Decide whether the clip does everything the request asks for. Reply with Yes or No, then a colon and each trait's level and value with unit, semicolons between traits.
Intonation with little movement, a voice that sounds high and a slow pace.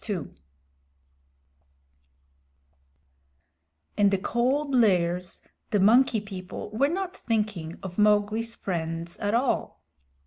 No: average, 4.5 semitones; high, 210 Hz; slow, 90 wpm